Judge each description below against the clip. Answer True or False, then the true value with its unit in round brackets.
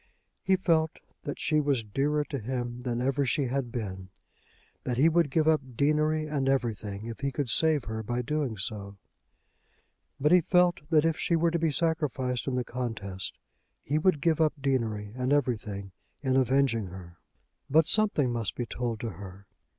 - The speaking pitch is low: True (130 Hz)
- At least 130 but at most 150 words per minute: False (180 wpm)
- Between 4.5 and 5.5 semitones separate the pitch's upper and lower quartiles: True (5.0 semitones)